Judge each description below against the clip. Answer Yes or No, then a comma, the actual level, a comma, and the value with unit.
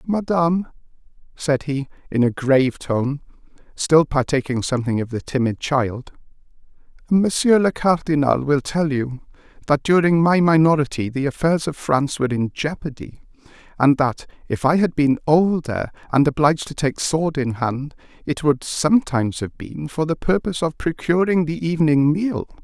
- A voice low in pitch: No, medium, 150 Hz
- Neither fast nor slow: Yes, average, 150 wpm